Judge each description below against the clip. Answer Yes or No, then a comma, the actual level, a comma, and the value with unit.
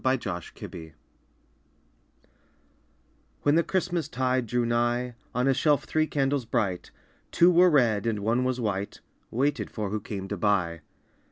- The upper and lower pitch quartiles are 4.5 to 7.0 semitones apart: Yes, average, 5.0 semitones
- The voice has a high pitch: No, low, 120 Hz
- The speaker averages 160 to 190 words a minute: No, average, 150 wpm